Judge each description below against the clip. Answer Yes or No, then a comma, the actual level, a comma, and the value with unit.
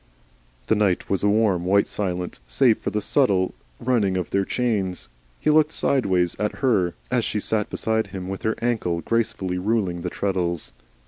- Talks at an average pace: Yes, average, 175 wpm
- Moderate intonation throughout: Yes, average, 3.5 semitones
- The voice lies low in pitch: Yes, low, 100 Hz